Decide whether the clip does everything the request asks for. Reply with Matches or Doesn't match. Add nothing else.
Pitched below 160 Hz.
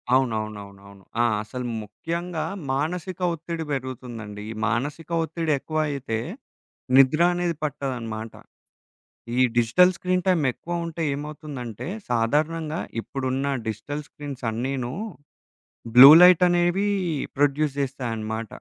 Matches